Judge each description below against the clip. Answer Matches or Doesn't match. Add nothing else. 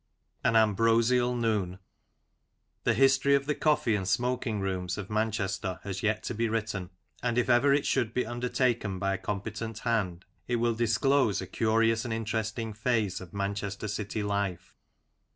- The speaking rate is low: Doesn't match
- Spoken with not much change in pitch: Doesn't match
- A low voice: Matches